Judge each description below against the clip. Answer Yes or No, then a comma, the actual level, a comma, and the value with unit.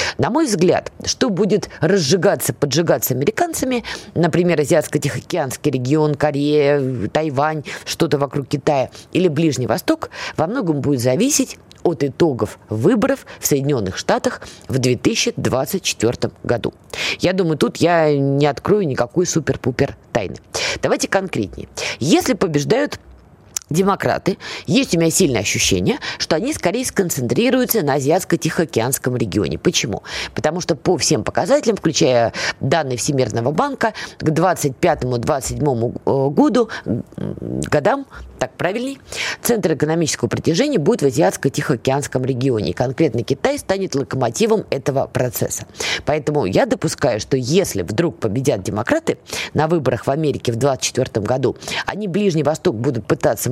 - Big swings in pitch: Yes, wide, 5.8 semitones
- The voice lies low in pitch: No, medium, 150 Hz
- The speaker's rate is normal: Yes, average, 120 wpm